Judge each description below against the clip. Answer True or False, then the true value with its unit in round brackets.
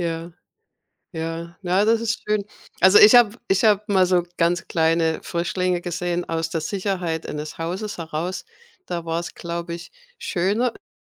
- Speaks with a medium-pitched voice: True (175 Hz)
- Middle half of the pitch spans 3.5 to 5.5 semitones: False (2.9 semitones)